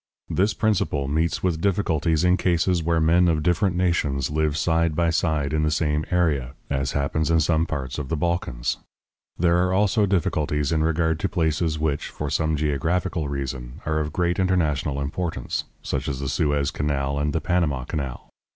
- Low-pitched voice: Yes, very low, 80 Hz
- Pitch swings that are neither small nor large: Yes, average, 3.1 semitones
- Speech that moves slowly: No, average, 180 wpm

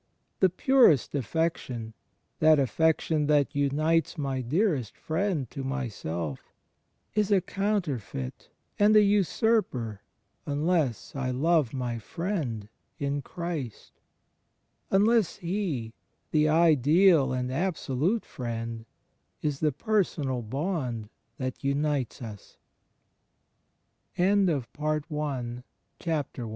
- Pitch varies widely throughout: Yes, wide, 5.7 semitones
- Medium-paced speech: No, slow, 90 wpm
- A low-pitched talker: No, medium, 145 Hz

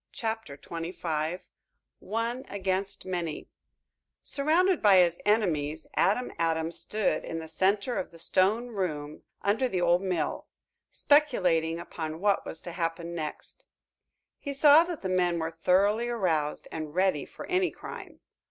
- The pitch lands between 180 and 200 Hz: Yes, medium, 185 Hz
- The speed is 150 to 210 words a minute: No, average, 140 wpm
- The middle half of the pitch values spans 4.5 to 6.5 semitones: Yes, average, 5.1 semitones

